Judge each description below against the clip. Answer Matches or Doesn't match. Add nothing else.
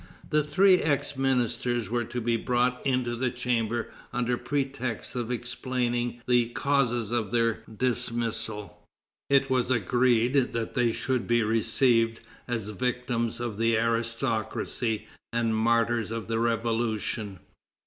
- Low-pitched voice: Matches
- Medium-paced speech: Doesn't match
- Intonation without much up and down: Matches